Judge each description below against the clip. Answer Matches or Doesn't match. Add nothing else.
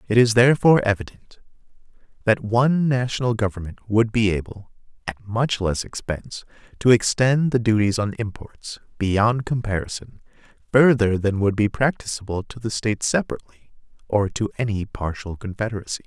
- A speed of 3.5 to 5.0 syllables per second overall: Doesn't match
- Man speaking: Matches